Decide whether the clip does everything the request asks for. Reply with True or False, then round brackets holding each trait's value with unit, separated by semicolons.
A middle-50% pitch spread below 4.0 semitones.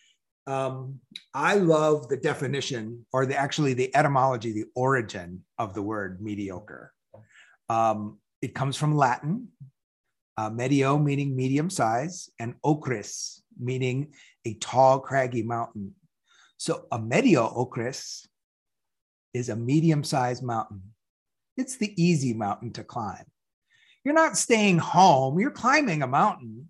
False (4.5 semitones)